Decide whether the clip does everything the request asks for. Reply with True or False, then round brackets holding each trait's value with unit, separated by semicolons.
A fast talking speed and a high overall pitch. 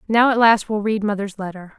True (235 wpm; 210 Hz)